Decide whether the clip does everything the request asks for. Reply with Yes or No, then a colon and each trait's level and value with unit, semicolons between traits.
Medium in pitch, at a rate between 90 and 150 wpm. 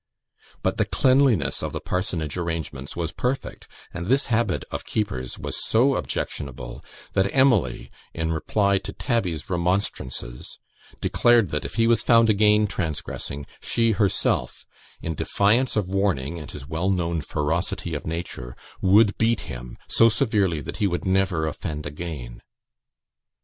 No: very low, 90 Hz; average, 145 wpm